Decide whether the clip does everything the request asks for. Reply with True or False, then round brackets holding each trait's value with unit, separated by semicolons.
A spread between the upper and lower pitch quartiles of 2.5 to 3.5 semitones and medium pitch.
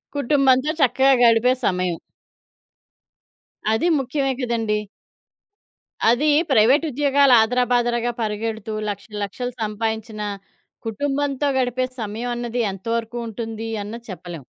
False (2.9 semitones; 235 Hz)